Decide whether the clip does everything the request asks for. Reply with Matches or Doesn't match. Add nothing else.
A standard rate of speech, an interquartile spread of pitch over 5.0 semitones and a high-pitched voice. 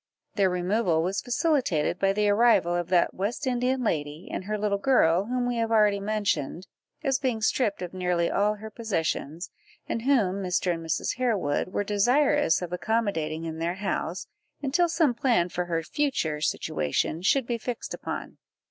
Matches